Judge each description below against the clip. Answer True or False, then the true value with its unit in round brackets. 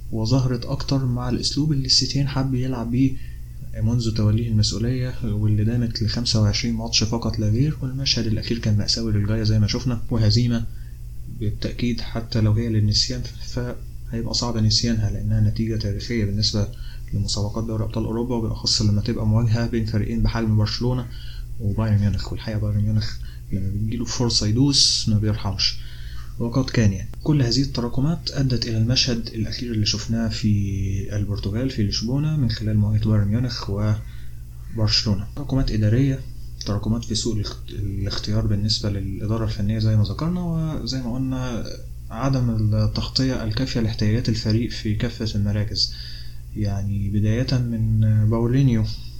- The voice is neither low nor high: False (110 Hz)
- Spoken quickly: True (140 wpm)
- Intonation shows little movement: True (2.3 semitones)